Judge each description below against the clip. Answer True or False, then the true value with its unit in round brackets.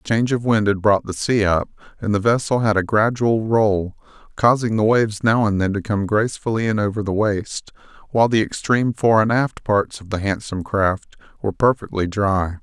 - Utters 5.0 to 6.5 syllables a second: True (5.4 syllables/s)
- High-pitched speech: False (105 Hz)